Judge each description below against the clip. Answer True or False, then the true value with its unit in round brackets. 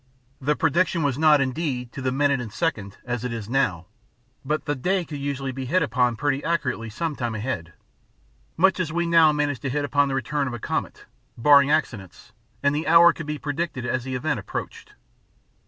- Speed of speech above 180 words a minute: True (200 wpm)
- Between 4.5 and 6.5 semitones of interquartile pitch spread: False (3.7 semitones)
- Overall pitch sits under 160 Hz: True (140 Hz)